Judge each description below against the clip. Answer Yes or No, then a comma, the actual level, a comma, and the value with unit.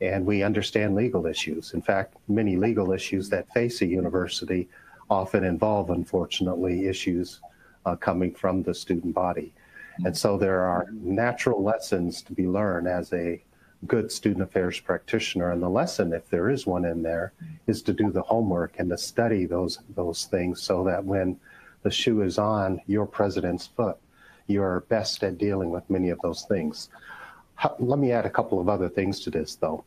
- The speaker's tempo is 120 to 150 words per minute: No, average, 180 wpm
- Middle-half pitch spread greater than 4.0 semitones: No, average, 2.7 semitones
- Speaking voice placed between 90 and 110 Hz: Yes, very low, 95 Hz